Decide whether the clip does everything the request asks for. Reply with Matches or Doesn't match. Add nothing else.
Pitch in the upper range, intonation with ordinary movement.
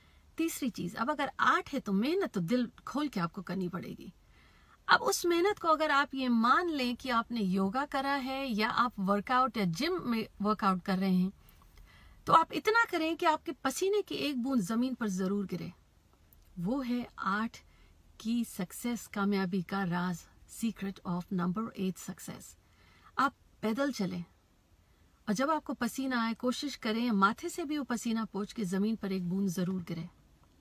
Doesn't match